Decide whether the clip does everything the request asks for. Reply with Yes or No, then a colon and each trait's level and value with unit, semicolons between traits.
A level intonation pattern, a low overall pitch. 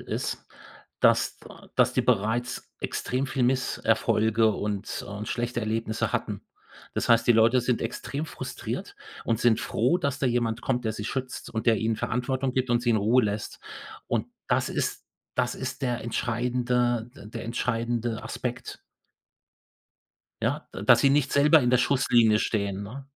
Yes: narrow, 2.3 semitones; low, 120 Hz